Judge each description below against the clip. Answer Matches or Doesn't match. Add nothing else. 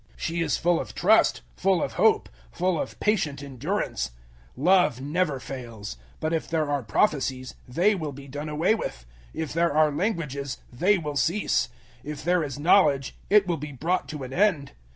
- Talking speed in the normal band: Matches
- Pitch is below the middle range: Doesn't match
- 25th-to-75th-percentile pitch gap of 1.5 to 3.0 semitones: Doesn't match